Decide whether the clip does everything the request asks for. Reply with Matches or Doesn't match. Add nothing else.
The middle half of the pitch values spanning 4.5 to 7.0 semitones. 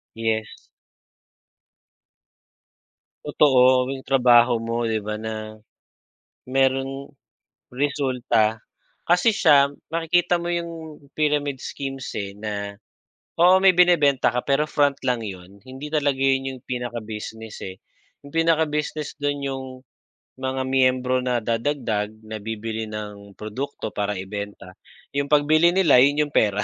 Matches